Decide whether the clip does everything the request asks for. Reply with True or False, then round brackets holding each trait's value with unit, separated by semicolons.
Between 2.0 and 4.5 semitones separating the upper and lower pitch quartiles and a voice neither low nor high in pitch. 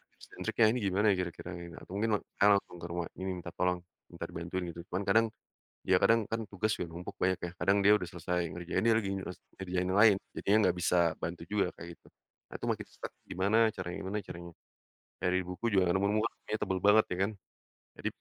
False (2.7 semitones; 95 Hz)